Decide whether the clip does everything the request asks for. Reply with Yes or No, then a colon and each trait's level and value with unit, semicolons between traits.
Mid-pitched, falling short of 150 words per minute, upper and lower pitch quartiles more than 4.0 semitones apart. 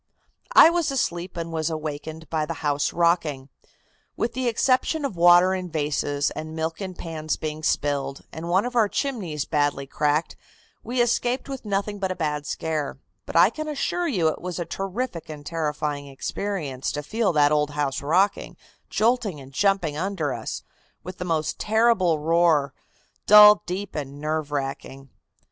No: medium, 165 Hz; average, 165 wpm; average, 5.2 semitones